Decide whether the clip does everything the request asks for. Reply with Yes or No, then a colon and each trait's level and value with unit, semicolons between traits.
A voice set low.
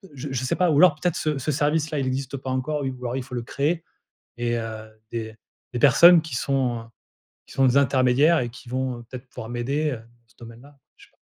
Yes: low, 130 Hz